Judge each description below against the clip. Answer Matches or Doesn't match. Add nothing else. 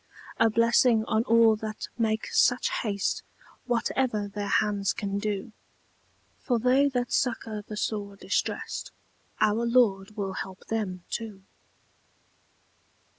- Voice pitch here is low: Doesn't match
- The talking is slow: Matches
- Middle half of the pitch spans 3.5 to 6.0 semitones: Doesn't match